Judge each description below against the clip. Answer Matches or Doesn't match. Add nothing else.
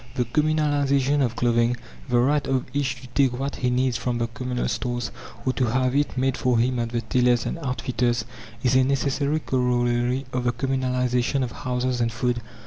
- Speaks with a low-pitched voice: Matches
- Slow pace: Doesn't match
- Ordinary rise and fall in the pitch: Doesn't match